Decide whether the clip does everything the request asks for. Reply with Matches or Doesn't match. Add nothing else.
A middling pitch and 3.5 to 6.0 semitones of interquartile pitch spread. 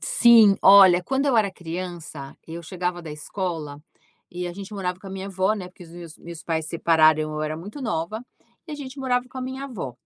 Matches